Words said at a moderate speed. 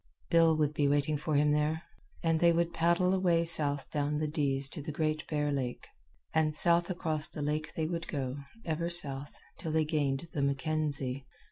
Yes: average, 190 wpm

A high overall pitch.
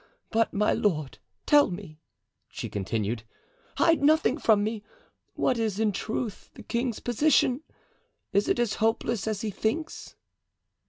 Yes: high, 220 Hz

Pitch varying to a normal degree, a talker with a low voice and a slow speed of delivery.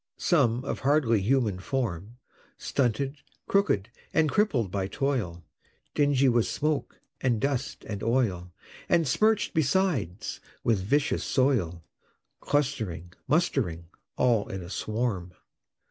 No: wide, 6.4 semitones; low, 120 Hz; slow, 115 wpm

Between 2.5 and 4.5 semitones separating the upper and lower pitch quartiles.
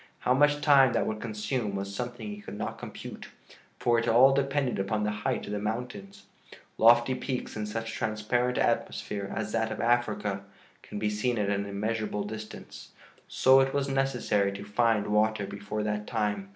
Yes: average, 3.0 semitones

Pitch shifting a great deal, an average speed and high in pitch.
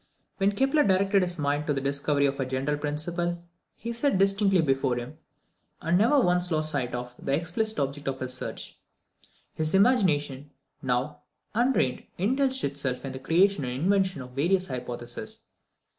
No: wide, 6.2 semitones; average, 160 wpm; medium, 155 Hz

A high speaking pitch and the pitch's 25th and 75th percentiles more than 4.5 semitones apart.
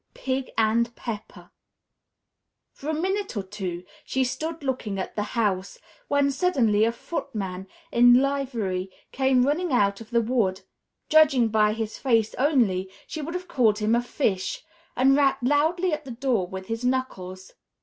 Yes: high, 240 Hz; average, 4.9 semitones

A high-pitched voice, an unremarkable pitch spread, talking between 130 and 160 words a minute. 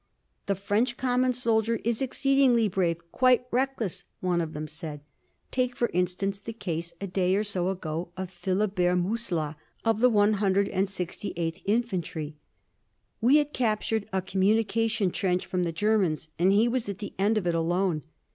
Yes: high, 195 Hz; average, 4.2 semitones; average, 155 wpm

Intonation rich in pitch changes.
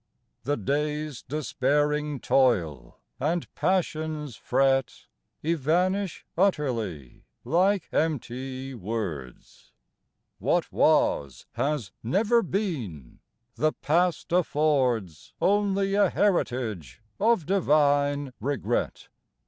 Yes: wide, 6.2 semitones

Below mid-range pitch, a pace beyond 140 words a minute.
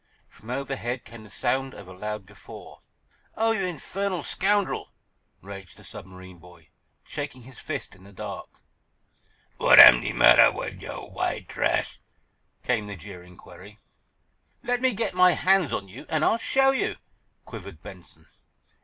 Yes: low, 125 Hz; average, 155 wpm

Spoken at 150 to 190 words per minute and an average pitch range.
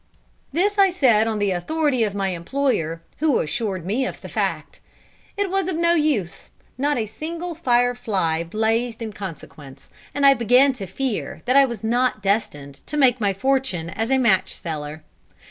No: average, 180 wpm; wide, 6.3 semitones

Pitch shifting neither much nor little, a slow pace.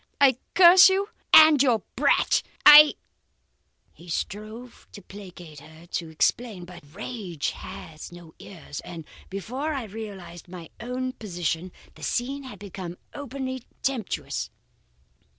No: wide, 6.9 semitones; slow, 125 wpm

